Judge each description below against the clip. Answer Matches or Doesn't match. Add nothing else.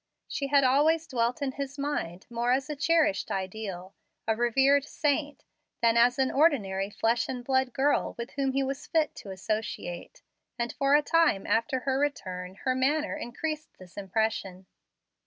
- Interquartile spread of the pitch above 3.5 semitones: Matches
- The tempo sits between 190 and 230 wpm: Doesn't match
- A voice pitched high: Matches